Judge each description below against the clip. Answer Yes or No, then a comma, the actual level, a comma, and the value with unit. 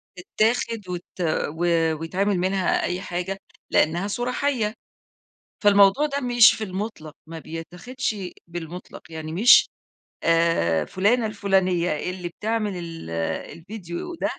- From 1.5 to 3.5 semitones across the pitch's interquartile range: No, average, 4.3 semitones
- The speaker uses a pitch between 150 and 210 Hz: Yes, high, 190 Hz